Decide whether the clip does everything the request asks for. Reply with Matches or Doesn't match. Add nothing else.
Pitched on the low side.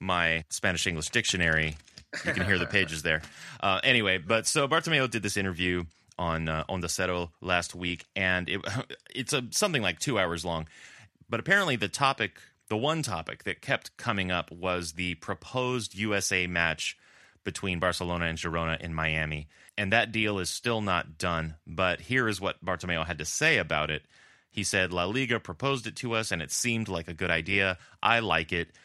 Matches